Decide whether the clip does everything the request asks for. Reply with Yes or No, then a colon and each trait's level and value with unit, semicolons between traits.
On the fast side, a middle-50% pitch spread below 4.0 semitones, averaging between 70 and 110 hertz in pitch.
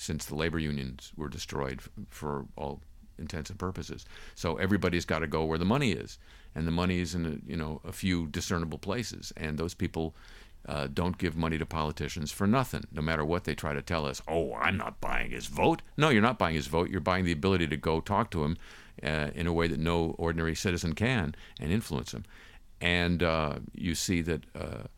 Yes: fast, 215 wpm; average, 2.7 semitones; very low, 85 Hz